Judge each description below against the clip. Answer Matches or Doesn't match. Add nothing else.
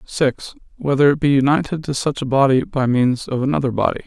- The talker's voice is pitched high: Doesn't match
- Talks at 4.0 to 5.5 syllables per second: Doesn't match